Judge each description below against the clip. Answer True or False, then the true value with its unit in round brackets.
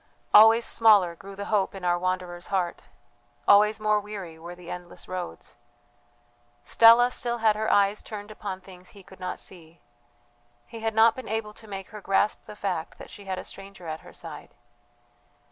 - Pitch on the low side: False (200 Hz)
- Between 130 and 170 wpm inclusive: False (180 wpm)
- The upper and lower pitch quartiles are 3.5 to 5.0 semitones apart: False (2.9 semitones)